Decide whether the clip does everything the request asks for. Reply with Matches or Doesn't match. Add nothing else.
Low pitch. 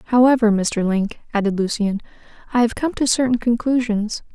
Doesn't match